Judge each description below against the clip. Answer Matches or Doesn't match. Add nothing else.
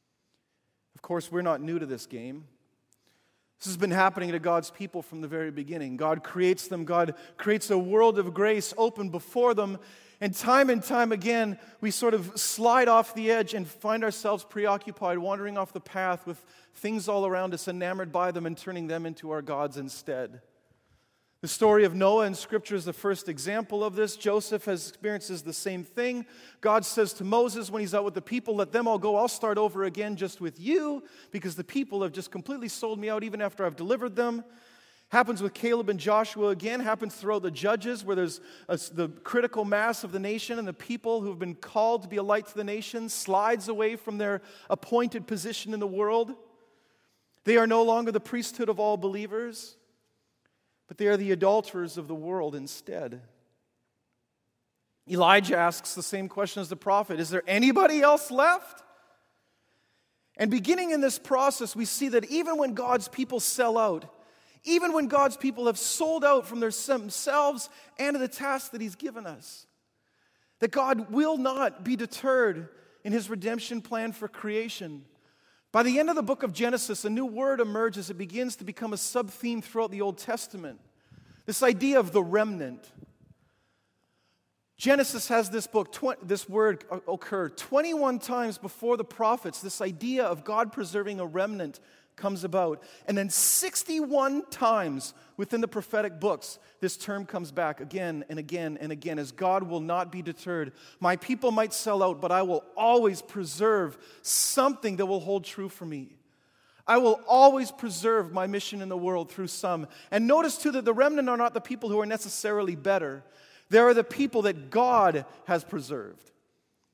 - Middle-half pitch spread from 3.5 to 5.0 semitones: Matches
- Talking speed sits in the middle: Matches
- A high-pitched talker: Matches